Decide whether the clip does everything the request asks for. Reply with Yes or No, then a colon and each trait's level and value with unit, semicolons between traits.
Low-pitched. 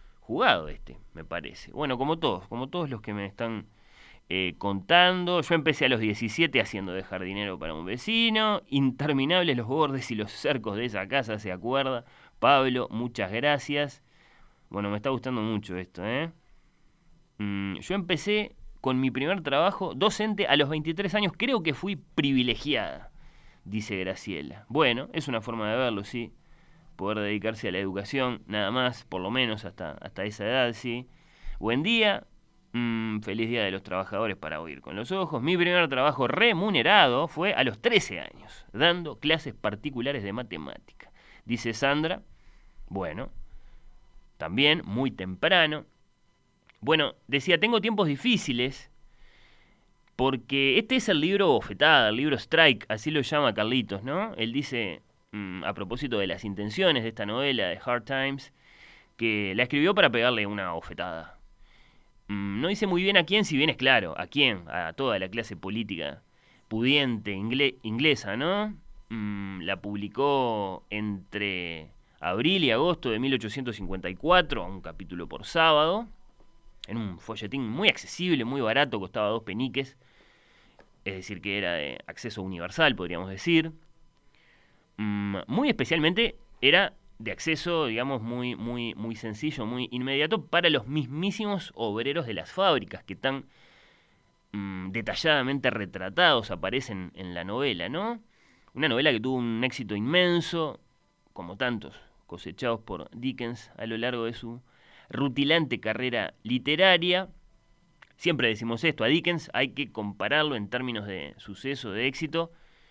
Yes: low, 125 Hz